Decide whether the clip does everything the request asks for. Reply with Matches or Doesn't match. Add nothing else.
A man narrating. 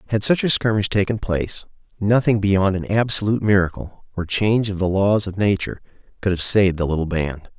Matches